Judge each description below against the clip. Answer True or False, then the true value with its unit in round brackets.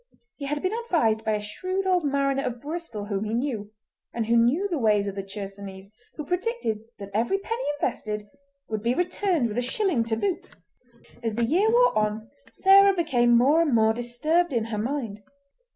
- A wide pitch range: True (7.9 semitones)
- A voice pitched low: False (240 Hz)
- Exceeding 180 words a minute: True (190 wpm)